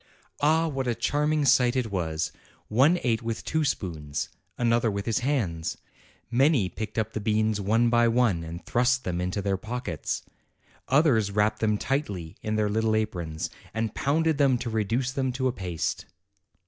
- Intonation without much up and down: No, average, 4.6 semitones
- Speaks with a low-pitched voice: Yes, low, 115 Hz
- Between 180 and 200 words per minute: No, average, 170 wpm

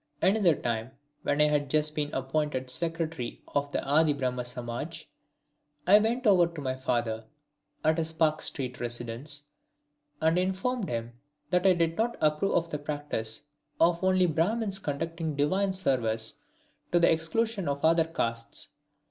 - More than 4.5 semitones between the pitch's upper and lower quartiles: Yes, average, 4.9 semitones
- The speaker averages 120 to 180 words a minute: Yes, average, 150 wpm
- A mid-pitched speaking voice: Yes, medium, 155 Hz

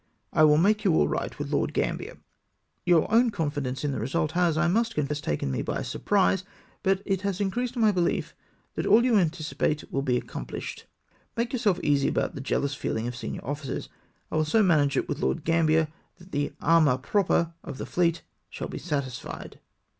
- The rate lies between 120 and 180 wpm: No, average, 190 wpm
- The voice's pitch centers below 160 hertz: No, medium, 165 Hz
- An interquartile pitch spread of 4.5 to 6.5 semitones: Yes, average, 5.3 semitones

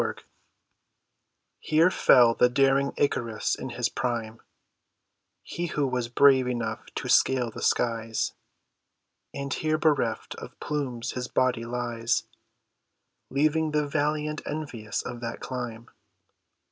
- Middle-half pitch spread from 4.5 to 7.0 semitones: No, average, 3.8 semitones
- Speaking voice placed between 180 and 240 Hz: No, low, 125 Hz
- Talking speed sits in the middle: No, slow, 120 wpm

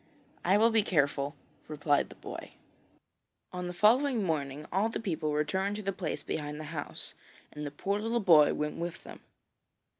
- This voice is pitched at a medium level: Yes, medium, 170 Hz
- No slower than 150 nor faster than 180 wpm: Yes, average, 175 wpm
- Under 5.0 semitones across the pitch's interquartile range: No, wide, 5.4 semitones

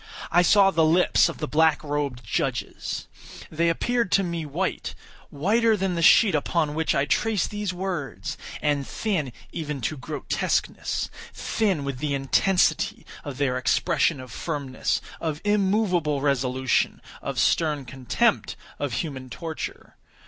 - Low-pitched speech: No, medium, 155 Hz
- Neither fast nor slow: No, slow, 125 wpm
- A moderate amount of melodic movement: Yes, average, 4.7 semitones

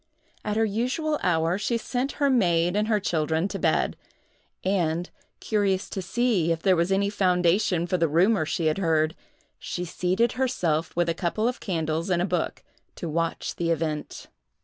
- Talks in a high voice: No, medium, 180 Hz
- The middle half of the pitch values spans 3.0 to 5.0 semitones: Yes, average, 4.1 semitones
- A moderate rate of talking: Yes, average, 175 wpm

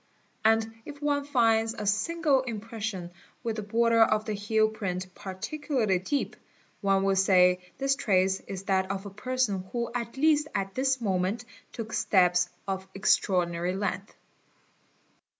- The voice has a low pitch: No, high, 215 Hz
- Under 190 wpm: Yes, average, 150 wpm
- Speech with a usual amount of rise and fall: Yes, average, 3.8 semitones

